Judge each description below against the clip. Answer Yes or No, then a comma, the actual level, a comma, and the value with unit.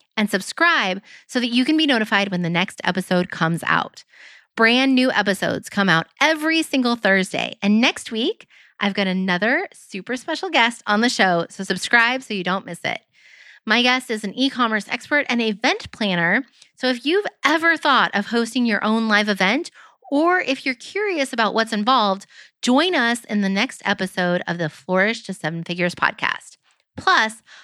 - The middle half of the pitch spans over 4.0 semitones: Yes, average, 5.3 semitones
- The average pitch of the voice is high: Yes, high, 225 Hz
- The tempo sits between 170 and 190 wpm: Yes, average, 180 wpm